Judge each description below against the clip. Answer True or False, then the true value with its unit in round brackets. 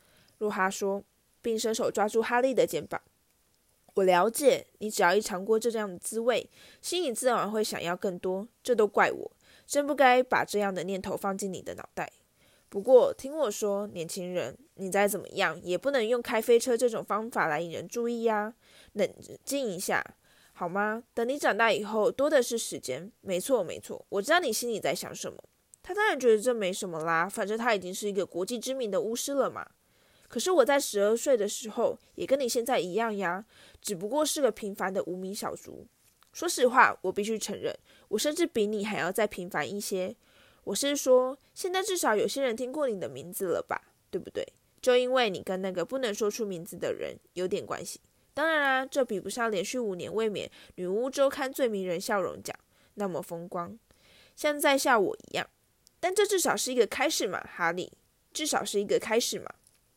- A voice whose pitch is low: False (220 Hz)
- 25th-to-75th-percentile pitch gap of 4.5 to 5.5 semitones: True (5.2 semitones)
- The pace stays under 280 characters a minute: False (290 characters per minute)